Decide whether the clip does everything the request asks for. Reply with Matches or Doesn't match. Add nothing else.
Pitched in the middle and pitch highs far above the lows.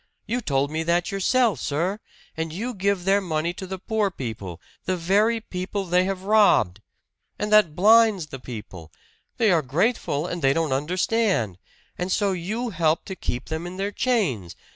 Doesn't match